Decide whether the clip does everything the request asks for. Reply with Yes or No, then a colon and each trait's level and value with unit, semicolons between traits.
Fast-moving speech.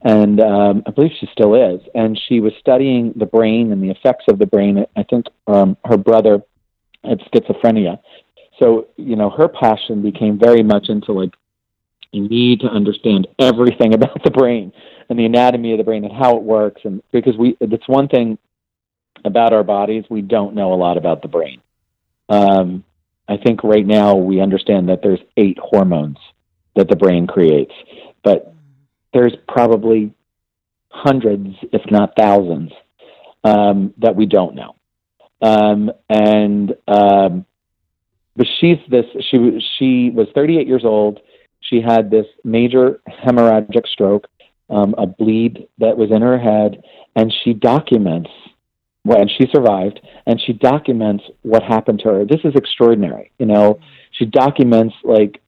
No: average, 160 wpm